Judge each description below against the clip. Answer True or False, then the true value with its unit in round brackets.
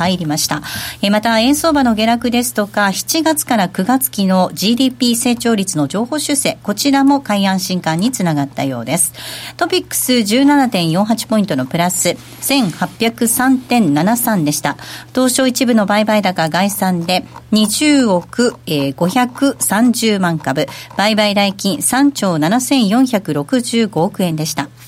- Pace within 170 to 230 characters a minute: True (220 characters per minute)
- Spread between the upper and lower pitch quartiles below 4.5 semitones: False (5.7 semitones)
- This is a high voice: True (215 Hz)